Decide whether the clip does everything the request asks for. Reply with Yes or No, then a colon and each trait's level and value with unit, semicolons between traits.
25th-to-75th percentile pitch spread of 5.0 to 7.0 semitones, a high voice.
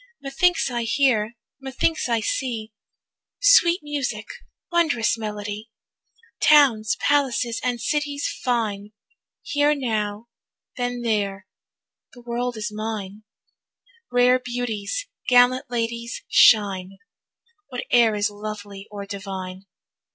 No: average, 3.4 semitones; high, 235 Hz